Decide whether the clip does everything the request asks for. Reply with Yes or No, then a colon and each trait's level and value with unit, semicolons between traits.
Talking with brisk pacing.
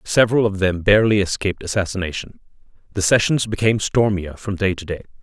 No: average, 160 wpm